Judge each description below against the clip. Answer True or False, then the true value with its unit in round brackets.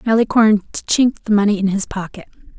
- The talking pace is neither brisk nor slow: True (165 wpm)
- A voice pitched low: False (210 Hz)